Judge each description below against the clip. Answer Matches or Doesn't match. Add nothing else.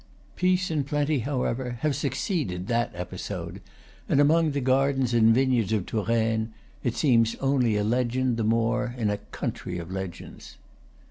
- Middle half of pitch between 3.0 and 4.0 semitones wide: Matches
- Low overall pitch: Matches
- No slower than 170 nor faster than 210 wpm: Doesn't match